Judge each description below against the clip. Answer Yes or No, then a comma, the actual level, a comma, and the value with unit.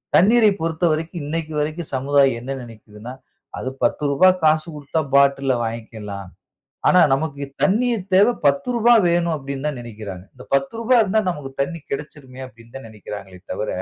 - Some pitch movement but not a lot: No, wide, 5.7 semitones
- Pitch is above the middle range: No, medium, 145 Hz